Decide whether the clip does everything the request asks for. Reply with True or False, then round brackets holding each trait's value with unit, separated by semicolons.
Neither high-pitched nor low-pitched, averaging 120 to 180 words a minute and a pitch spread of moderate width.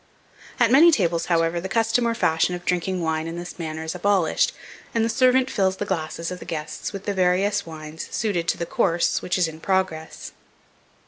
False (180 Hz; 200 wpm; 3.7 semitones)